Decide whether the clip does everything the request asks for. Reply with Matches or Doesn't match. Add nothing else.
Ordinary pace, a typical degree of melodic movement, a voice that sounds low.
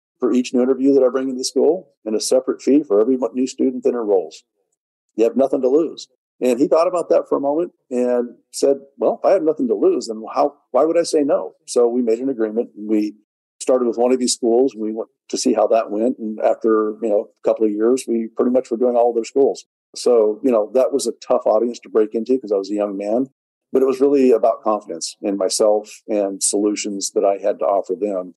Doesn't match